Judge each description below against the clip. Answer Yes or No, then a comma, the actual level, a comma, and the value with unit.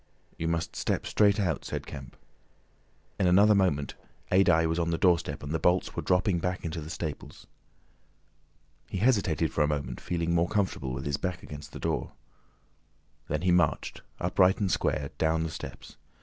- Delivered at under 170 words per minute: No, average, 175 wpm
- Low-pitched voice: Yes, very low, 85 Hz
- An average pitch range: Yes, average, 3.1 semitones